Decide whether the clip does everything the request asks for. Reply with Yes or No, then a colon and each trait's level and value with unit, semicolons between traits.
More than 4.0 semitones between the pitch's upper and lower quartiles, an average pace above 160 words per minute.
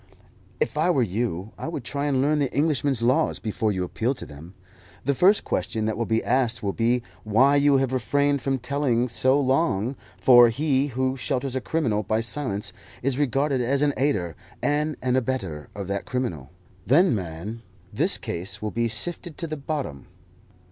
Yes: average, 4.4 semitones; average, 180 wpm